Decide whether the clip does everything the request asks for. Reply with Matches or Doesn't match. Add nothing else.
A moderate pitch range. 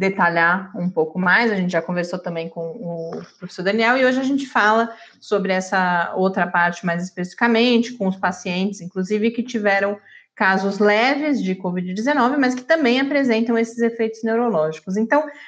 Matches